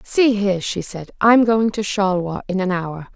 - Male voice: No, female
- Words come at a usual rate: No, fast, 210 wpm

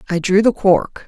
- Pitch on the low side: No, high, 190 Hz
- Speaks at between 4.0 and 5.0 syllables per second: Yes, 4.6 syllables/s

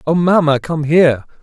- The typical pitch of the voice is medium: Yes, medium, 155 Hz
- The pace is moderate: Yes, average, 170 wpm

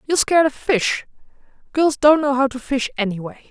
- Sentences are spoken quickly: No, average, 190 wpm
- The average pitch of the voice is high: Yes, very high, 270 Hz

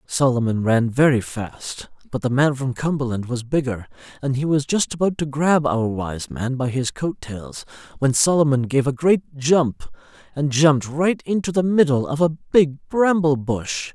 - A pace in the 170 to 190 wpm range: Yes, average, 180 wpm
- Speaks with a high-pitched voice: No, medium, 140 Hz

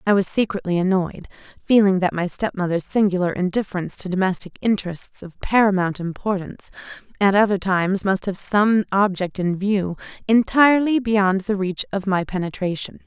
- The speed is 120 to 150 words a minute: Yes, average, 145 wpm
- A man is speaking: No, female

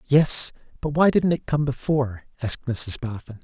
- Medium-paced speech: Yes, average, 175 wpm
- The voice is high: No, low, 130 Hz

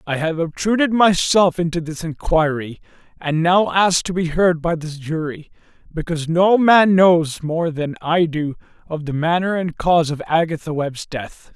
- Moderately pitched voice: Yes, medium, 165 Hz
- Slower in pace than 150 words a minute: No, average, 170 wpm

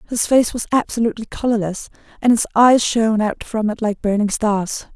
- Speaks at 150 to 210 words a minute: Yes, average, 180 wpm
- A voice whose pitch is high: Yes, high, 220 Hz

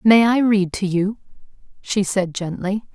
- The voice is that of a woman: Yes, female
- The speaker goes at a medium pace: Yes, average, 165 wpm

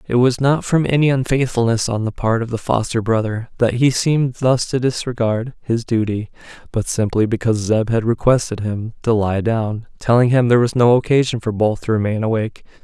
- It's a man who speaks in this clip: Yes, male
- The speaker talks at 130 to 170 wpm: No, average, 190 wpm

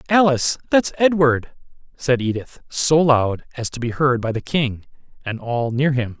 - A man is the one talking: Yes, male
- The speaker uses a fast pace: No, average, 175 wpm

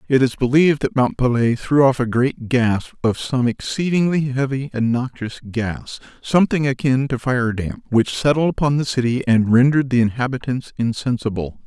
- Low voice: Yes, low, 130 Hz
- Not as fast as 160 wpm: No, average, 165 wpm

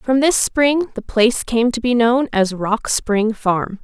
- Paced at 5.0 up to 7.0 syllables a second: No, 3.8 syllables/s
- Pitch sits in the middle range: No, high, 235 Hz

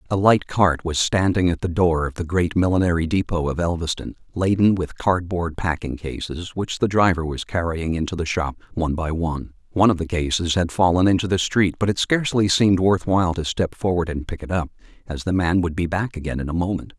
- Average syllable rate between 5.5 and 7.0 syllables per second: Yes, 5.7 syllables/s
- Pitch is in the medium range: No, very low, 90 Hz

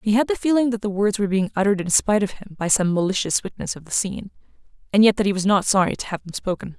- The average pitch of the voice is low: No, high, 200 Hz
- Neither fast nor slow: No, fast, 285 wpm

